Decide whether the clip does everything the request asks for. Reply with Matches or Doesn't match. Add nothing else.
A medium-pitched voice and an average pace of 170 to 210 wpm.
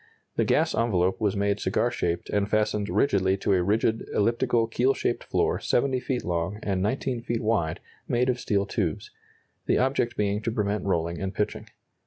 Doesn't match